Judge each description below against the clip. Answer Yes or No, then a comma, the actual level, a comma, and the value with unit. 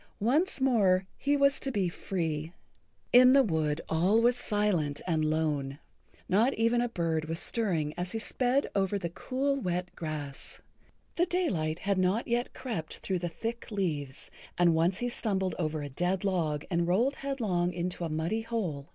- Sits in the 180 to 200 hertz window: Yes, medium, 185 Hz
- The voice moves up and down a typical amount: No, wide, 6.4 semitones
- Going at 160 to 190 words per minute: Yes, average, 170 wpm